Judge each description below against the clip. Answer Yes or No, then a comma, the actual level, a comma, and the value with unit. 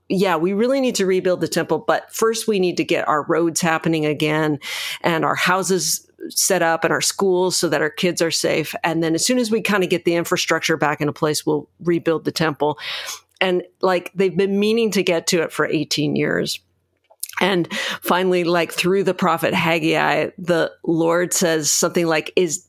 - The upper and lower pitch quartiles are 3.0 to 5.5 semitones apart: No, narrow, 2.5 semitones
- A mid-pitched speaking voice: Yes, medium, 175 Hz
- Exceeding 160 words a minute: Yes, average, 200 wpm